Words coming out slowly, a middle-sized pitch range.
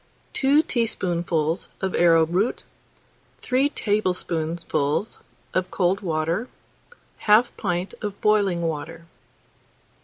Yes: slow, 85 wpm; average, 4.2 semitones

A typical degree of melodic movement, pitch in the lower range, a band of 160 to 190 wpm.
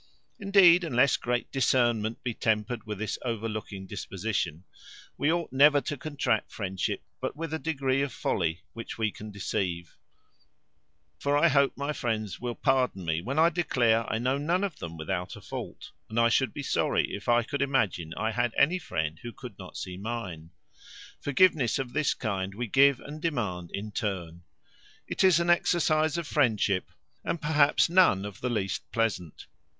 No: wide, 6.4 semitones; low, 120 Hz; average, 175 wpm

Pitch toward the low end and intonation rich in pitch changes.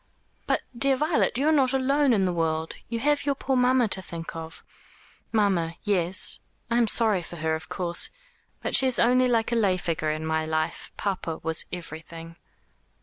No: high, 190 Hz; wide, 7.4 semitones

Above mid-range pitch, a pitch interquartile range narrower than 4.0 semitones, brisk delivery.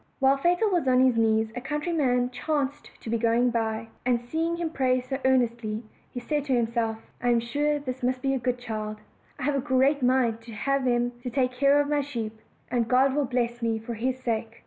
Yes: very high, 250 Hz; average, 2.9 semitones; fast, 215 wpm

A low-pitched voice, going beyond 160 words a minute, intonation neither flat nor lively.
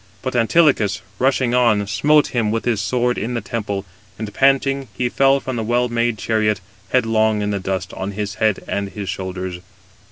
Yes: low, 110 Hz; average, 185 wpm; average, 3.5 semitones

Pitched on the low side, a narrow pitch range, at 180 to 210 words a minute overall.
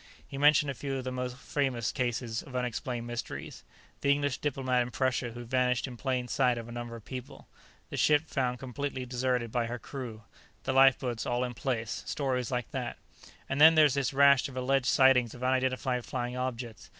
Yes: low, 125 Hz; narrow, 1.8 semitones; average, 190 wpm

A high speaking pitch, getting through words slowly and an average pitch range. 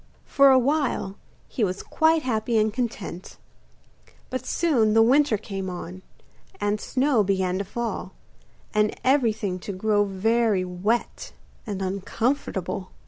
Yes: high, 215 Hz; slow, 130 wpm; average, 4.4 semitones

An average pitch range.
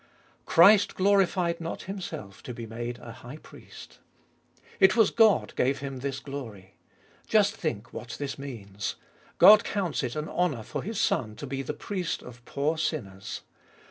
No: wide, 7.3 semitones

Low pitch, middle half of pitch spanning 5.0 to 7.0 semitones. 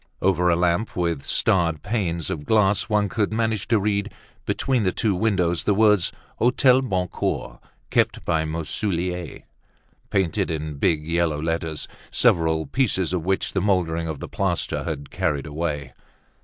No: very low, 90 Hz; average, 4.1 semitones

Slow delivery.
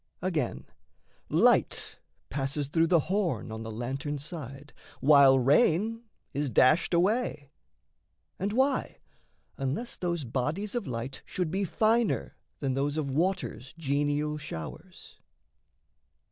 Yes: slow, 115 wpm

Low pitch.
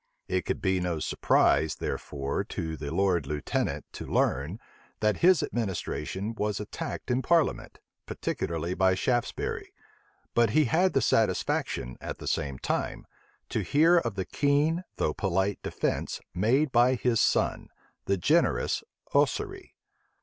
Yes: low, 105 Hz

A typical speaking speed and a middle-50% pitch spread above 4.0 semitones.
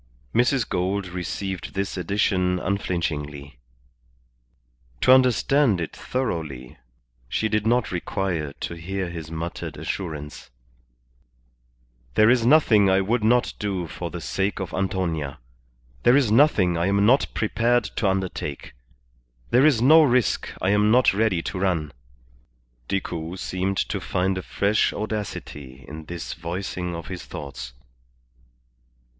No: slow, 130 wpm; average, 4.5 semitones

